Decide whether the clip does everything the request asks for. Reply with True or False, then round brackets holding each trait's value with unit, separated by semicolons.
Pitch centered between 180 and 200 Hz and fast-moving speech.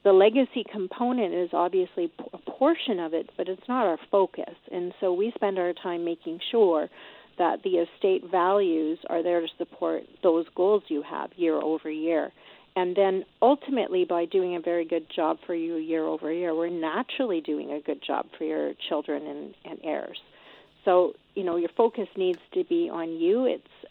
False (185 Hz; 185 wpm)